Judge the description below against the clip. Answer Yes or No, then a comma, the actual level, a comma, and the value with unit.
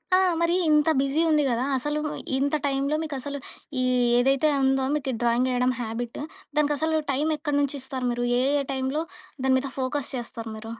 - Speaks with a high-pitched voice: Yes, very high, 270 Hz